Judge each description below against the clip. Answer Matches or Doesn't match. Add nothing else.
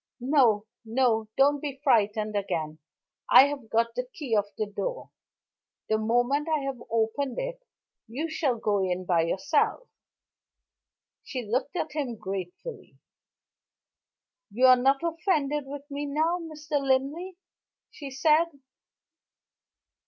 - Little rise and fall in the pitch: Doesn't match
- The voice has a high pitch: Matches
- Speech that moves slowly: Matches